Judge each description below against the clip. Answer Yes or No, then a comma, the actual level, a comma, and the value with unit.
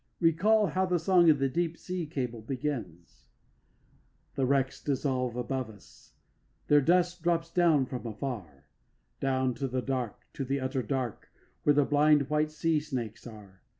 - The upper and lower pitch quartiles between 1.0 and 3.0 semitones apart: No, average, 4.4 semitones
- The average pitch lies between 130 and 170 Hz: Yes, low, 135 Hz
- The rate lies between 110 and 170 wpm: Yes, average, 155 wpm